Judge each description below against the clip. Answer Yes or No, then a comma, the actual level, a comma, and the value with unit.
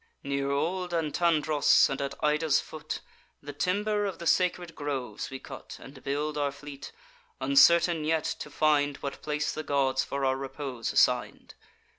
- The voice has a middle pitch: Yes, medium, 150 Hz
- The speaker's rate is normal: Yes, average, 155 wpm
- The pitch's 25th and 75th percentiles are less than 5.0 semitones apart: Yes, average, 2.9 semitones